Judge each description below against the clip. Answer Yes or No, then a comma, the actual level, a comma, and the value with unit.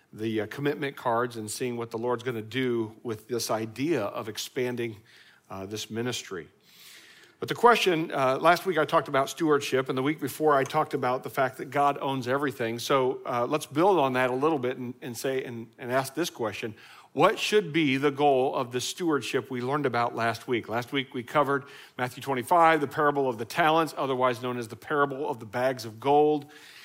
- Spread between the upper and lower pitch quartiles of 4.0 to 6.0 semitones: No, average, 3.2 semitones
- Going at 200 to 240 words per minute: Yes, fast, 205 wpm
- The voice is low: Yes, low, 130 Hz